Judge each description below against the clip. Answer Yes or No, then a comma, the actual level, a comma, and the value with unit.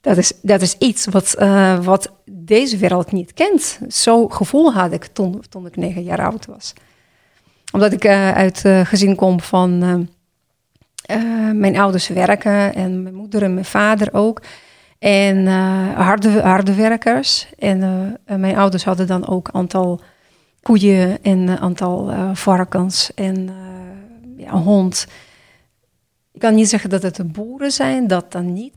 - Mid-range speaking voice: No, high, 195 Hz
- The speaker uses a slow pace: No, average, 165 wpm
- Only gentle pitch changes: Yes, narrow, 2.3 semitones